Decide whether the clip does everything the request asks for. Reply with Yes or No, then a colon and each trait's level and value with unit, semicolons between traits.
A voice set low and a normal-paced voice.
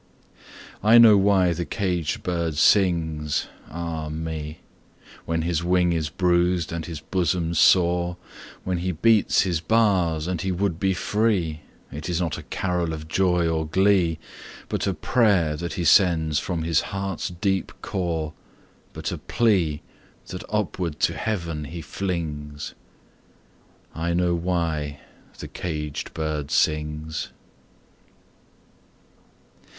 No: very low, 85 Hz; slow, 130 wpm